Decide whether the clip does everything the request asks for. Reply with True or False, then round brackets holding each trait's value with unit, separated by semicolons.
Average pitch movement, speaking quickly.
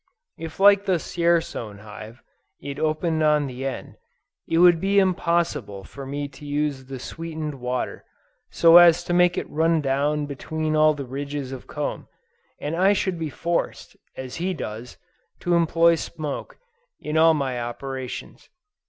False (3.8 semitones; 155 wpm)